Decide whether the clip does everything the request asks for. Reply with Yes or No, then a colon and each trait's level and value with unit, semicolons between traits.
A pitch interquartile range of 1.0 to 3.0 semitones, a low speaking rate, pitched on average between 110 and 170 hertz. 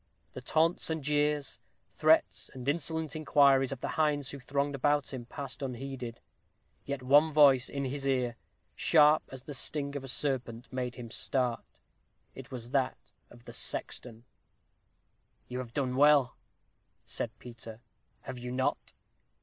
No: narrow, 2.5 semitones; average, 150 wpm; low, 135 Hz